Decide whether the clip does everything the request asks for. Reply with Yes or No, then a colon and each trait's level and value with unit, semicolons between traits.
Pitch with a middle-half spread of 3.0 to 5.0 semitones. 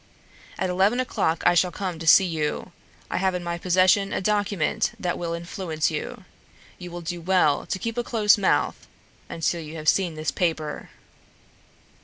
No: narrow, 2.6 semitones